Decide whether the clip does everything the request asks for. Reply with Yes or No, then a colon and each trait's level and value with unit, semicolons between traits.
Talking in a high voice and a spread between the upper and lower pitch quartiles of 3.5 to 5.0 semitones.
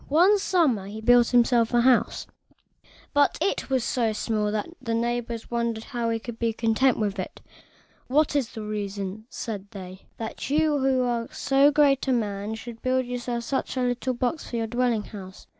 No: high, 235 Hz; average, 3.0 semitones